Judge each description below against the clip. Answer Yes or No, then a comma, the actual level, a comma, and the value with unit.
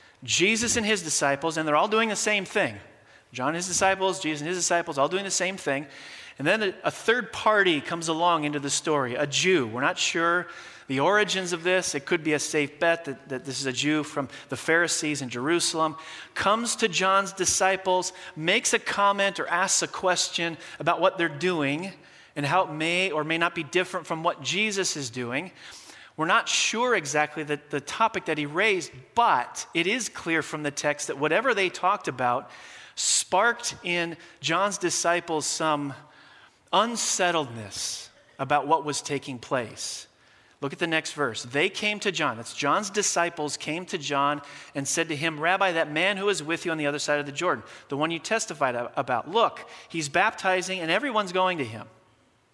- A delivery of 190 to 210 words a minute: Yes, average, 195 wpm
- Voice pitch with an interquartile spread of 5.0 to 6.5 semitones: No, average, 4.2 semitones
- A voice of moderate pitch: Yes, medium, 170 Hz